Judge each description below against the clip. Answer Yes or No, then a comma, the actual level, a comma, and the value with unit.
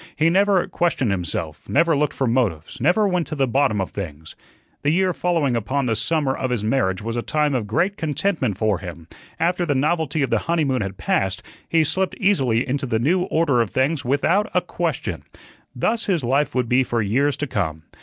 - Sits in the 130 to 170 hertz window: Yes, low, 135 Hz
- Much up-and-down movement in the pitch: Yes, wide, 6.6 semitones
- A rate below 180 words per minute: No, fast, 205 wpm